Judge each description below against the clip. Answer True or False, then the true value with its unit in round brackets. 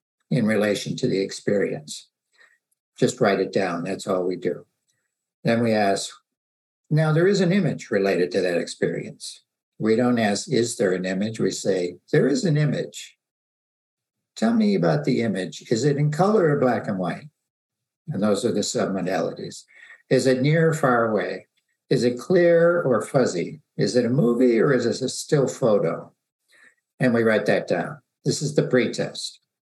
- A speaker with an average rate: True (175 wpm)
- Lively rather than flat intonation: True (7.5 semitones)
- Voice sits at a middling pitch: False (125 Hz)